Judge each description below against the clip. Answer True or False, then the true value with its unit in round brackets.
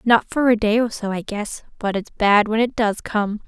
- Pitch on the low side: False (215 Hz)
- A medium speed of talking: False (260 wpm)